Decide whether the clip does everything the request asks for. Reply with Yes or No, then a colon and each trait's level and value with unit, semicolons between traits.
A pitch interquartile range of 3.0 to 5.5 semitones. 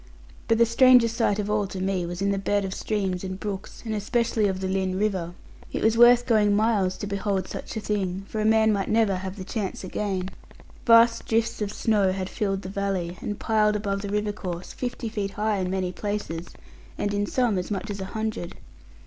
No: narrow, 2.5 semitones